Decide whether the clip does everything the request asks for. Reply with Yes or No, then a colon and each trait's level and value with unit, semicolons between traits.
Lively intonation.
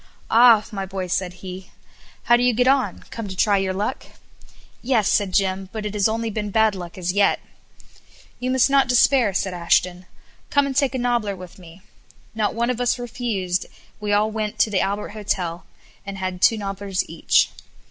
No: average, 3.8 semitones